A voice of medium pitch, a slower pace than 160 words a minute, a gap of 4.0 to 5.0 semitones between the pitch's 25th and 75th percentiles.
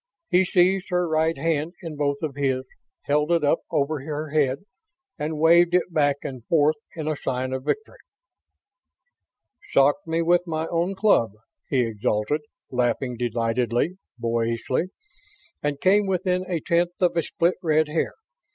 Yes: medium, 155 Hz; average, 150 wpm; average, 4.4 semitones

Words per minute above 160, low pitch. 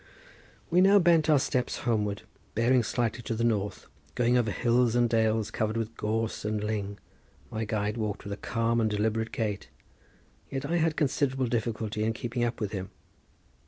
Yes: average, 175 wpm; low, 115 Hz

